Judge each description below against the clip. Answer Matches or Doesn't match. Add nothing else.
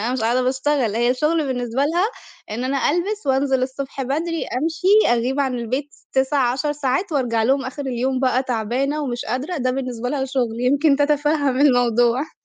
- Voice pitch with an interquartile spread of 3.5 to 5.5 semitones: Doesn't match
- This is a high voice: Matches